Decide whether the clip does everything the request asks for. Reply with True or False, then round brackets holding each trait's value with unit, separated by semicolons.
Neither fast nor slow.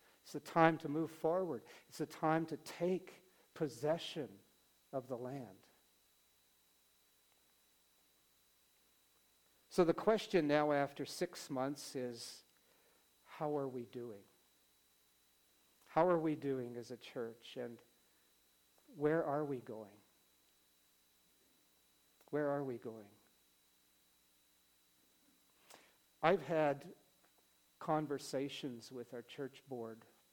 False (100 wpm)